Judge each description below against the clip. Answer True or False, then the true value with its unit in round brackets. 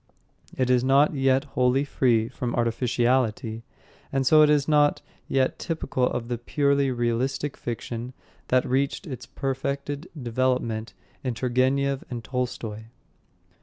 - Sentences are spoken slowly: True (125 wpm)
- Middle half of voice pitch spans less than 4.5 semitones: True (2.5 semitones)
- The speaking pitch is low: True (130 Hz)